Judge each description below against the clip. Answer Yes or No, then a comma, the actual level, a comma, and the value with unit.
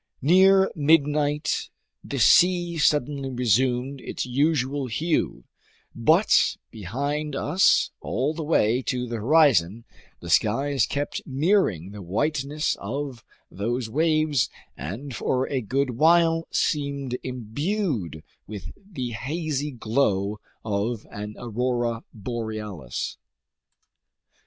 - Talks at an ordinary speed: No, slow, 105 wpm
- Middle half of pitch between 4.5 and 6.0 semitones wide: Yes, average, 4.9 semitones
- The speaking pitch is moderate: No, low, 130 Hz